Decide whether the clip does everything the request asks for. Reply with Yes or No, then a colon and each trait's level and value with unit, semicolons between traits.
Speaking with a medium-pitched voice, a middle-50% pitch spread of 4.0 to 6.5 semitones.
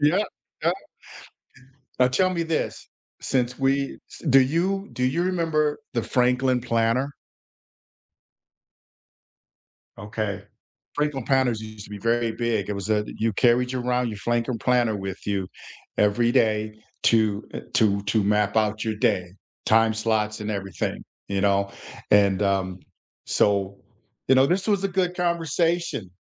No: low, 115 Hz; average, 4.5 semitones